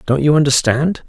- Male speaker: Yes, male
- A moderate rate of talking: Yes, average, 165 wpm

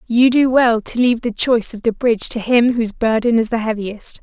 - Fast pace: Yes, fast, 240 wpm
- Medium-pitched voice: No, high, 230 Hz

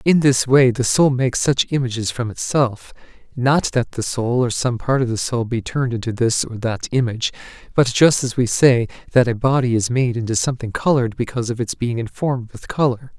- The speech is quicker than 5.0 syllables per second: Yes, 5.5 syllables/s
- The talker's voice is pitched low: Yes, low, 120 Hz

